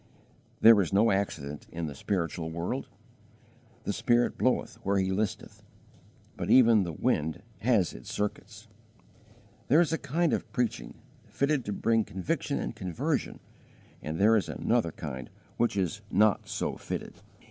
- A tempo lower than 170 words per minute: Yes, average, 145 wpm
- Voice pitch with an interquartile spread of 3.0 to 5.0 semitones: No, wide, 5.6 semitones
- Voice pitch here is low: Yes, low, 100 Hz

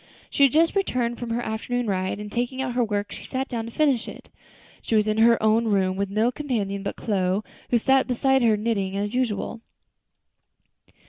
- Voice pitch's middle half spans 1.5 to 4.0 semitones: Yes, average, 3.3 semitones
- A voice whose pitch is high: Yes, high, 230 Hz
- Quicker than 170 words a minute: Yes, average, 200 wpm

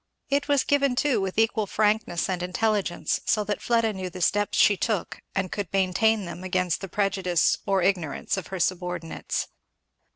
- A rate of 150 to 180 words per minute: Yes, average, 175 wpm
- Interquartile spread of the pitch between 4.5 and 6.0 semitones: No, average, 3.1 semitones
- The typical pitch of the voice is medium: No, high, 195 Hz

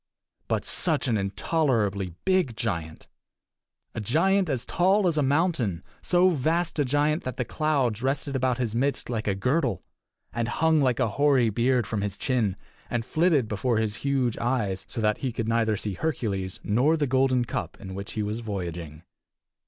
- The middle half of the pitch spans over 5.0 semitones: Yes, wide, 5.5 semitones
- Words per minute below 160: No, average, 175 wpm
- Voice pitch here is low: Yes, low, 120 Hz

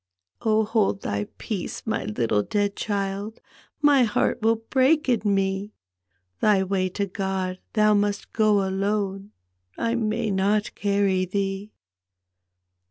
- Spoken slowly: Yes, slow, 130 wpm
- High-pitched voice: Yes, high, 205 Hz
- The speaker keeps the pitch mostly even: Yes, narrow, 2.0 semitones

